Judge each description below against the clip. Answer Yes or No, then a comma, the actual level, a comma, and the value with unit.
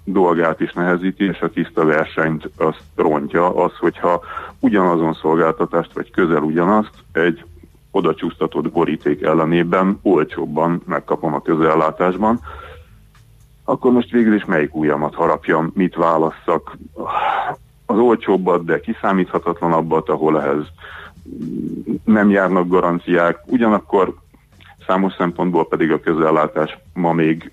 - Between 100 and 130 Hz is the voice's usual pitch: No, very low, 85 Hz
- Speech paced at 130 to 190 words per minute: No, slow, 105 wpm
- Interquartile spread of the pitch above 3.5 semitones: No, average, 3.0 semitones